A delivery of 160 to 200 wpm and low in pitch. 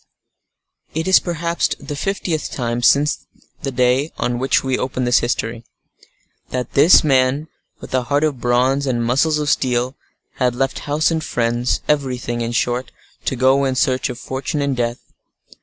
Yes: average, 165 wpm; low, 130 Hz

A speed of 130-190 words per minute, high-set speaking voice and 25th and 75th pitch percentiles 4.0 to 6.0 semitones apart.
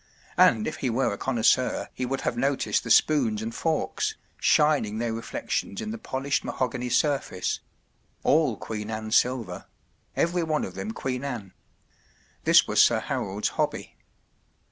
No: average, 145 wpm; low, 125 Hz; average, 4.7 semitones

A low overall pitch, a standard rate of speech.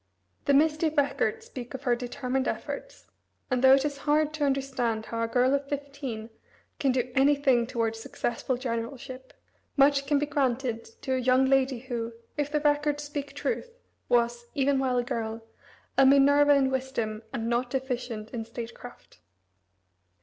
No: very high, 265 Hz; average, 165 wpm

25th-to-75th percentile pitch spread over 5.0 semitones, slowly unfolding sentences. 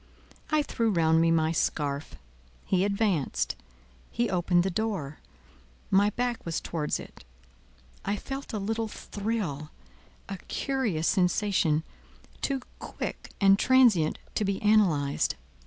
Yes: wide, 5.5 semitones; slow, 120 wpm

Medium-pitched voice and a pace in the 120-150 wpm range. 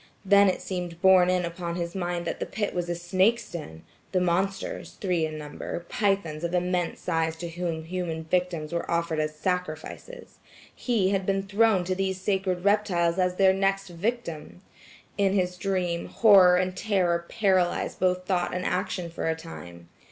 No: medium, 180 Hz; average, 165 wpm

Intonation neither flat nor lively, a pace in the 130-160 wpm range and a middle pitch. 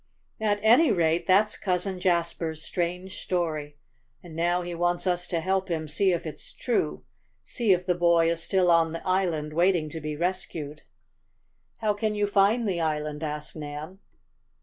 No: average, 3.0 semitones; average, 170 wpm; medium, 175 Hz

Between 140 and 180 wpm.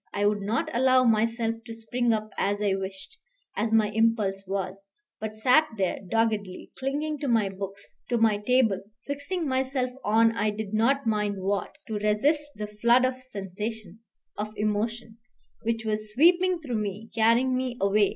Yes: average, 165 wpm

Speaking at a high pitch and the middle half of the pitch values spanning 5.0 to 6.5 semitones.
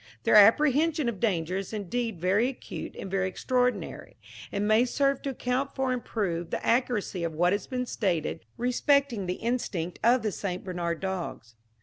Yes: high, 215 Hz; wide, 5.4 semitones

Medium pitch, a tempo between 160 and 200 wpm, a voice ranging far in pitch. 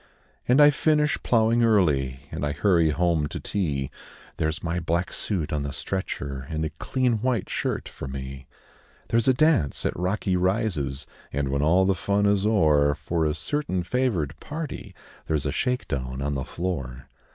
No: very low, 85 Hz; average, 175 wpm; wide, 6.9 semitones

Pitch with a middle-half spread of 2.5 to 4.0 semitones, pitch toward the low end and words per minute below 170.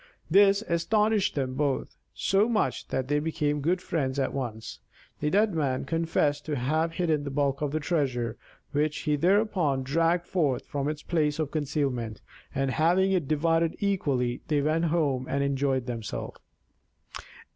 No: average, 3.6 semitones; medium, 150 Hz; average, 155 wpm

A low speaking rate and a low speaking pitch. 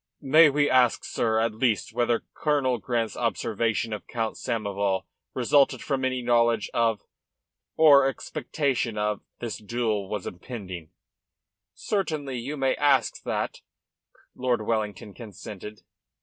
Yes: slow, 125 wpm; low, 115 Hz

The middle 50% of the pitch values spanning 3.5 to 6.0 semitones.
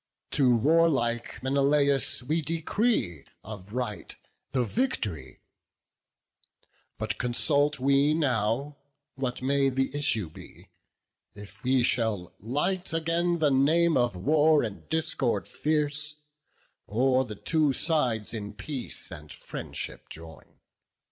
Yes: average, 5.1 semitones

